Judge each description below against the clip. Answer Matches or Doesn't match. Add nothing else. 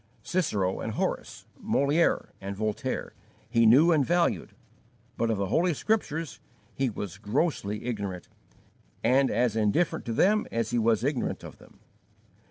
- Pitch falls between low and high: Doesn't match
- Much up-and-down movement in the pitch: Matches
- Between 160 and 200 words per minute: Doesn't match